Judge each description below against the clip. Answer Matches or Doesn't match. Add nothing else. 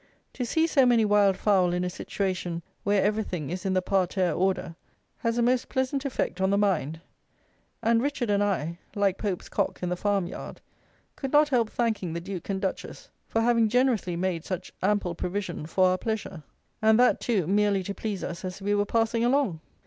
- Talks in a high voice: Matches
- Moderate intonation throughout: Matches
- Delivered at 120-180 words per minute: Doesn't match